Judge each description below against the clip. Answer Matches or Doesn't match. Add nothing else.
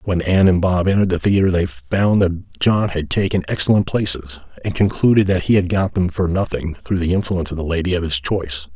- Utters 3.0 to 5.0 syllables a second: Doesn't match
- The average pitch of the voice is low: Matches